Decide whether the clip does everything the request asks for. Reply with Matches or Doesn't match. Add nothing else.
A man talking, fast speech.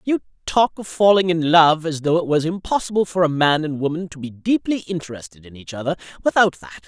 Matches